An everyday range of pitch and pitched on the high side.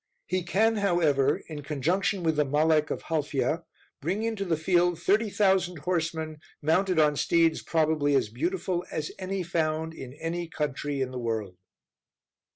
No: average, 3.4 semitones; medium, 160 Hz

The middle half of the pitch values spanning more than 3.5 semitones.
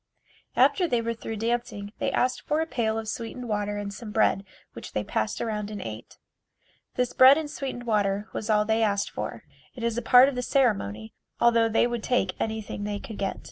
No: average, 2.8 semitones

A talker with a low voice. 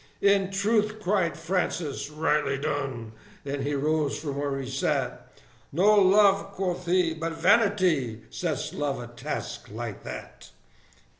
No: medium, 165 Hz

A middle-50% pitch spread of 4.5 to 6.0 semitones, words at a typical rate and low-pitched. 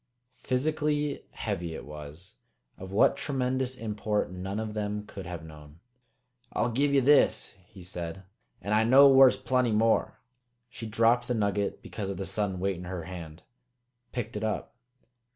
Yes: wide, 5.4 semitones; average, 155 wpm; low, 105 Hz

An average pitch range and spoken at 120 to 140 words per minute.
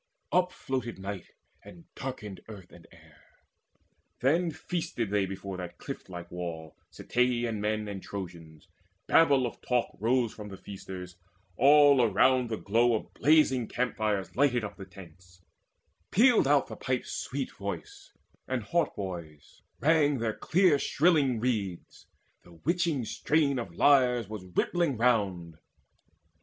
No: wide, 6.4 semitones; slow, 135 wpm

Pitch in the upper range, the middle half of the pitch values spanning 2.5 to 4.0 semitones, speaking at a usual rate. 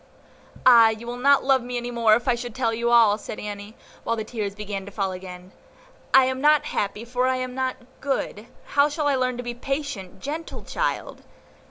No: high, 240 Hz; average, 3.4 semitones; fast, 215 wpm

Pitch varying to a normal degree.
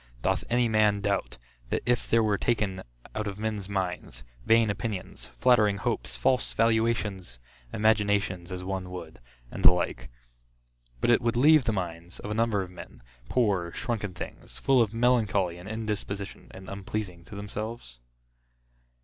Yes: average, 3.3 semitones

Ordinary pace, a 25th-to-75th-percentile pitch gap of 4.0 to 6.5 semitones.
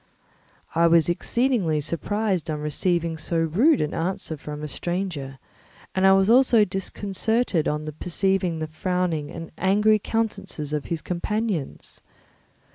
No: slow, 130 wpm; average, 4.3 semitones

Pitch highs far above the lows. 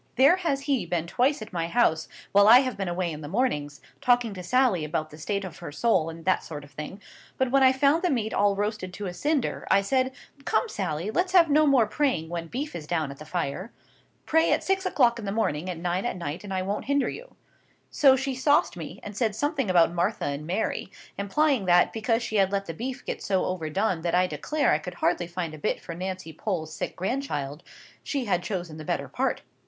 Yes: wide, 7.2 semitones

